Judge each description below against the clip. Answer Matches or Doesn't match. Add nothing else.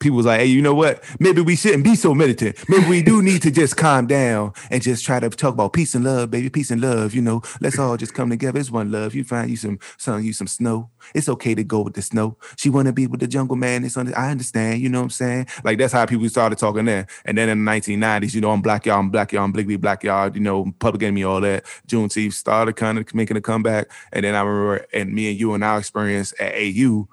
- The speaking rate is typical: Doesn't match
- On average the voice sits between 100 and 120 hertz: Matches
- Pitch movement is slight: Doesn't match